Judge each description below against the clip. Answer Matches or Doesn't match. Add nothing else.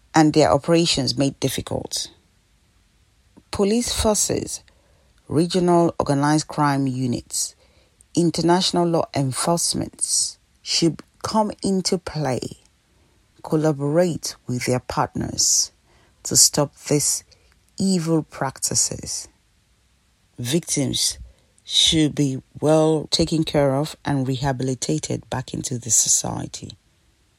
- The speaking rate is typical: Doesn't match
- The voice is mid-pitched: Matches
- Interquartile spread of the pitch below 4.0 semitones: Doesn't match